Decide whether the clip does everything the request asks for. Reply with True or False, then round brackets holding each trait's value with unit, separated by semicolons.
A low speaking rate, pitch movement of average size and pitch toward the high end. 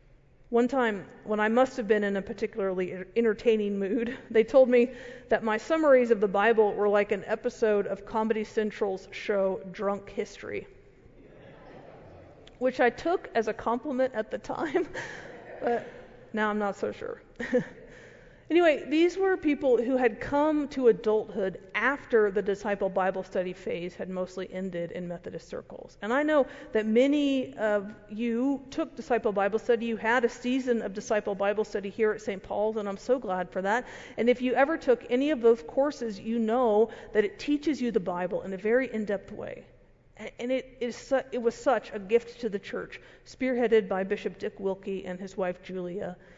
False (180 wpm; 3.8 semitones; 225 Hz)